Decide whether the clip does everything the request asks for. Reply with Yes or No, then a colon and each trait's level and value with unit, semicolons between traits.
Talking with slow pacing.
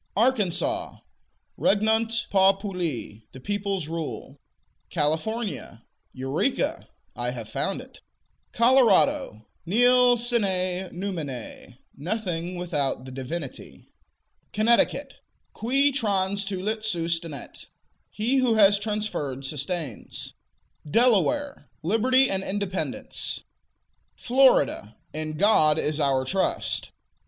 Yes: slow, 85 wpm